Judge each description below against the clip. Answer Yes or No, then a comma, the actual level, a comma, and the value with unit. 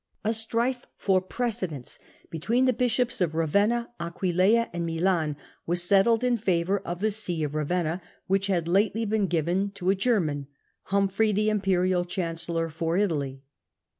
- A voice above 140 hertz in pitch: Yes, high, 190 Hz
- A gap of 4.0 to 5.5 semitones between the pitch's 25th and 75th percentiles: Yes, average, 4.3 semitones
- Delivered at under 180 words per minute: Yes, average, 150 wpm